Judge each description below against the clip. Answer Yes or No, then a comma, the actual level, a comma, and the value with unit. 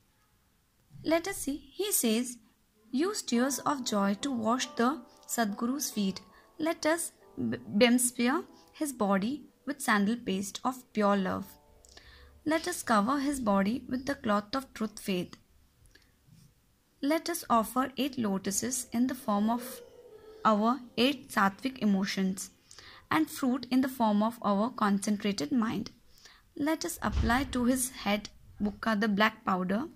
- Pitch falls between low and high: No, high, 245 Hz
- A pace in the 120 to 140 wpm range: Yes, average, 135 wpm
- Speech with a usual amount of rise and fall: Yes, average, 4.7 semitones